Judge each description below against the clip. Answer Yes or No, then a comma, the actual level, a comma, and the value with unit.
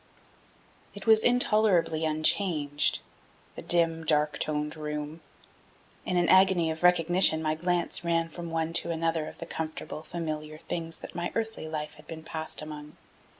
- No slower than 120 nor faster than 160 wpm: Yes, average, 150 wpm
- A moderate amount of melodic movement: No, narrow, 2.1 semitones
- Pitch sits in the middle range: Yes, medium, 165 Hz